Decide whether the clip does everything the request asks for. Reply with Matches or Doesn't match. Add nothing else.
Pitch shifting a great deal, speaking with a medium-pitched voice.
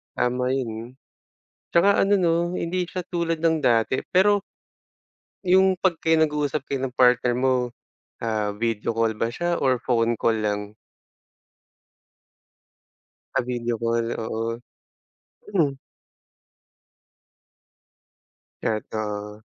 Doesn't match